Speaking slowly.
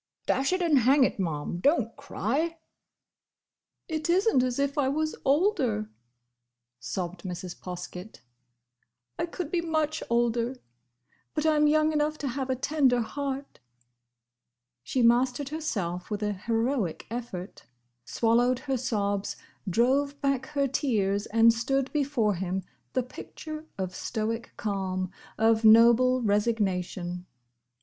Yes: slow, 125 wpm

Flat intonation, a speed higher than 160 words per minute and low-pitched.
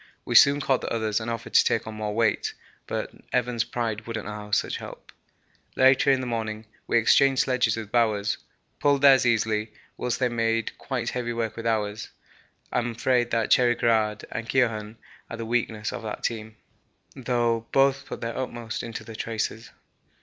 Yes: narrow, 2.0 semitones; average, 180 wpm; low, 115 Hz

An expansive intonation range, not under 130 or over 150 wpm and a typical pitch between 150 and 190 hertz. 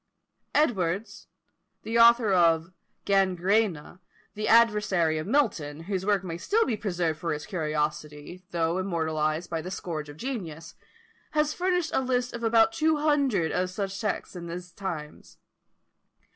Yes: wide, 5.7 semitones; average, 145 wpm; medium, 185 Hz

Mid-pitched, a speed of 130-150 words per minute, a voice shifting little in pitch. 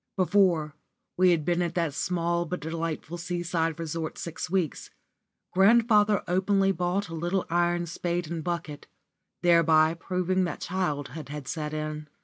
Yes: medium, 170 Hz; average, 145 wpm; narrow, 2.2 semitones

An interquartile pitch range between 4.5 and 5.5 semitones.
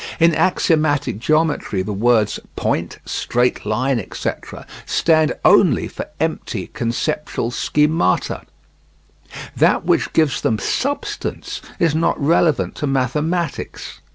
Yes: average, 5.1 semitones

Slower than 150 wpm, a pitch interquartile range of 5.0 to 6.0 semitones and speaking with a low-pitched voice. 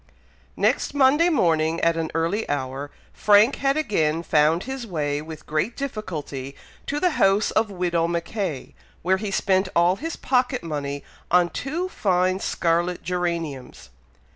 No: average, 140 wpm; wide, 5.4 semitones; medium, 180 Hz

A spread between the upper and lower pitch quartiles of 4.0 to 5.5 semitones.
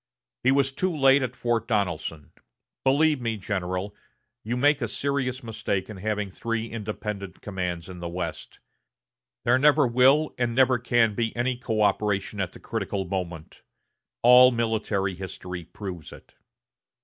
Yes: average, 4.9 semitones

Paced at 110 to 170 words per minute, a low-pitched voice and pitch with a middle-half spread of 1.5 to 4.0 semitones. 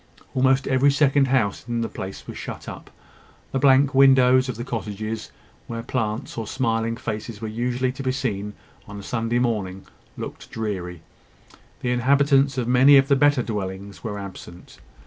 Yes: average, 165 wpm; low, 120 Hz; average, 3.7 semitones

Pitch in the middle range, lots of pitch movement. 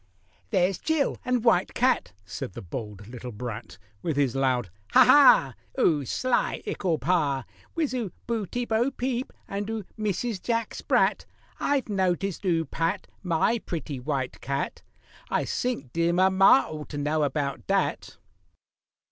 Yes: medium, 180 Hz; wide, 8.5 semitones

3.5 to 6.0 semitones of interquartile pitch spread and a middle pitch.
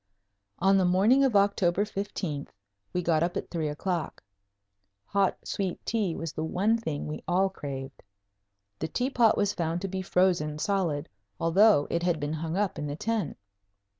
Yes: average, 4.0 semitones; medium, 180 Hz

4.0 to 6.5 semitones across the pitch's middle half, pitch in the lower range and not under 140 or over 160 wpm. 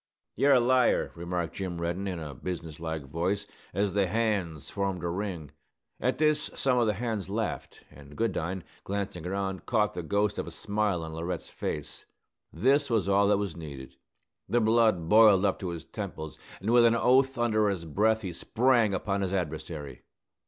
No: average, 4.6 semitones; very low, 95 Hz; average, 180 wpm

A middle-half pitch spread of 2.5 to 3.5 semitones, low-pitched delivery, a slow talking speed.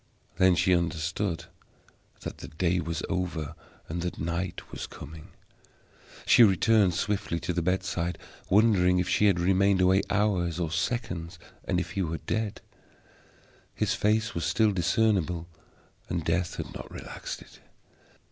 No: average, 2.8 semitones; very low, 90 Hz; average, 145 wpm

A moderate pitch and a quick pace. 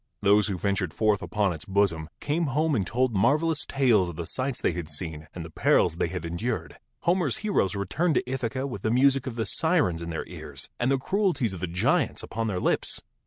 No: low, 110 Hz; fast, 215 wpm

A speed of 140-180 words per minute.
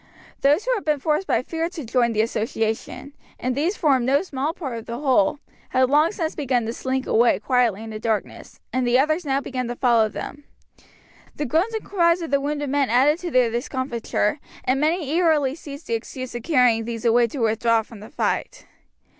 No: fast, 205 wpm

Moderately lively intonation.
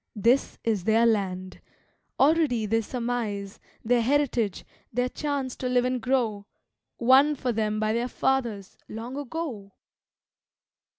Yes: average, 3.4 semitones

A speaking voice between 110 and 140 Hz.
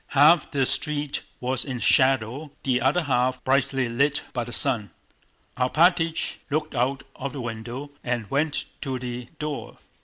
Yes: low, 135 Hz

